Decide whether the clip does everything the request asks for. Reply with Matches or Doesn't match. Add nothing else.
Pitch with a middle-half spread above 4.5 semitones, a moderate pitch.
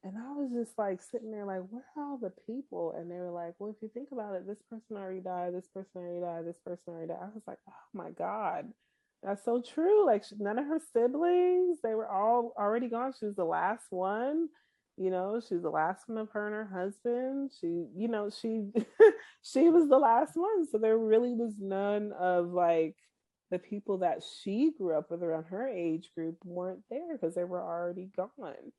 Doesn't match